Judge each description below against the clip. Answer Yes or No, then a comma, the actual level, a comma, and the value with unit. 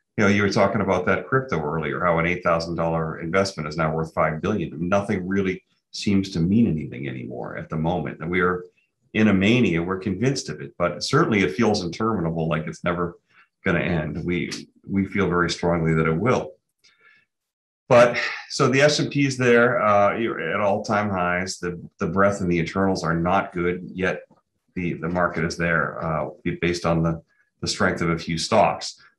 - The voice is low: Yes, very low, 90 Hz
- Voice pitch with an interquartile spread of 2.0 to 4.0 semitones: Yes, average, 3.3 semitones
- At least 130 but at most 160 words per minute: No, average, 190 wpm